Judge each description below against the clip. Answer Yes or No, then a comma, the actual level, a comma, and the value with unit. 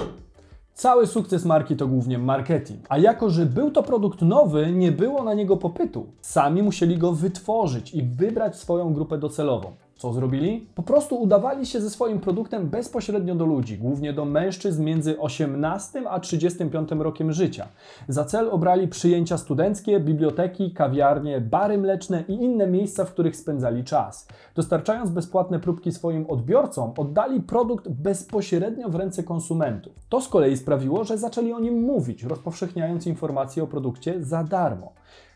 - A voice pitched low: No, medium, 175 Hz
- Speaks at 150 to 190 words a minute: Yes, average, 155 wpm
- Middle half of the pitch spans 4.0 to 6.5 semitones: Yes, average, 4.8 semitones